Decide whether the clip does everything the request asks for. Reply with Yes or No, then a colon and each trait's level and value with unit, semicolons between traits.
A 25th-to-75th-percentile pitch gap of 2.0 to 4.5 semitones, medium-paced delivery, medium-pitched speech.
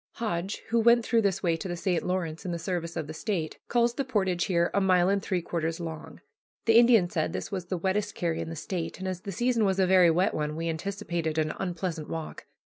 No: average, 3.2 semitones; fast, 240 wpm; medium, 180 Hz